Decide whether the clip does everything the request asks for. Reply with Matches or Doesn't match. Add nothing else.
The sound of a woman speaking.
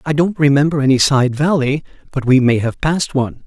Doesn't match